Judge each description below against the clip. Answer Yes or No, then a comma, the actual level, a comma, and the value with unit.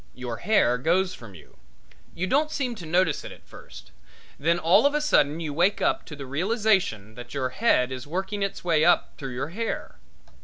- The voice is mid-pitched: Yes, medium, 165 Hz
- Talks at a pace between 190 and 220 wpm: Yes, average, 200 wpm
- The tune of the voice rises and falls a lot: Yes, wide, 7.0 semitones